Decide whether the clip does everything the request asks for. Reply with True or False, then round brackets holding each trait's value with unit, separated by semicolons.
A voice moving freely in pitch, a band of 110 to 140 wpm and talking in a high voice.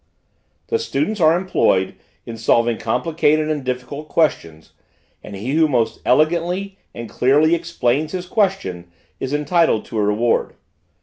False (6.3 semitones; 135 wpm; 150 Hz)